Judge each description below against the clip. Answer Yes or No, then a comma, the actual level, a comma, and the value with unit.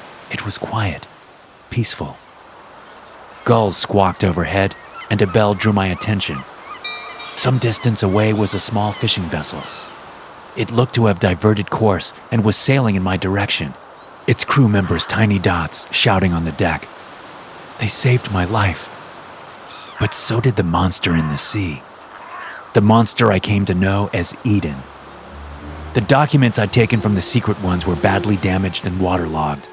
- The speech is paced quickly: No, average, 150 wpm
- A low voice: Yes, low, 100 Hz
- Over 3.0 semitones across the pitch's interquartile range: Yes, average, 3.7 semitones